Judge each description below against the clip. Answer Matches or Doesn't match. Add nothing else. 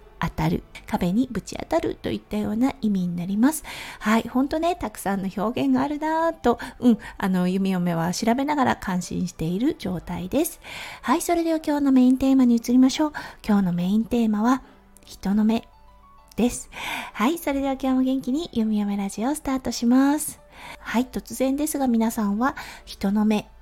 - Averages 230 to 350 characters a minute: Doesn't match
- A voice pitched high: Matches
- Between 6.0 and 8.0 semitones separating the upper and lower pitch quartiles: Doesn't match